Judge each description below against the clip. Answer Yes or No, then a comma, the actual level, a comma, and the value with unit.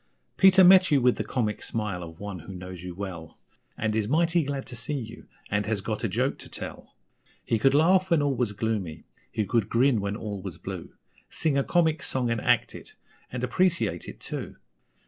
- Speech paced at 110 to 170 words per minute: No, fast, 205 wpm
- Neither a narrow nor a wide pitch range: No, wide, 6.0 semitones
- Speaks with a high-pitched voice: No, low, 115 Hz